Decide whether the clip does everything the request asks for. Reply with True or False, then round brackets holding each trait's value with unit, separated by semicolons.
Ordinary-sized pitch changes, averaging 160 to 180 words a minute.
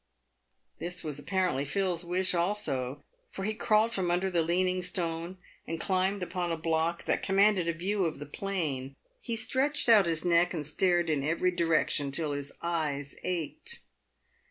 True (3.0 semitones; 165 wpm)